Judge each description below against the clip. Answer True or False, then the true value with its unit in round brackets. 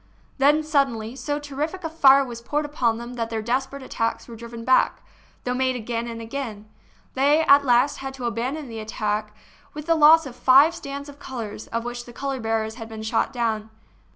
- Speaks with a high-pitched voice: True (250 Hz)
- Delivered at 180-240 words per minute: True (200 wpm)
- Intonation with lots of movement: False (3.5 semitones)